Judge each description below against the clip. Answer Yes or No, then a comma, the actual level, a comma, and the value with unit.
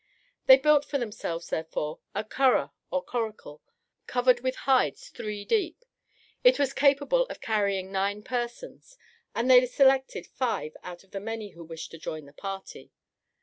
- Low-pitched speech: No, high, 235 Hz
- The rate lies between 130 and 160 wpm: Yes, average, 155 wpm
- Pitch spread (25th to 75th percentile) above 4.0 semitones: Yes, wide, 5.6 semitones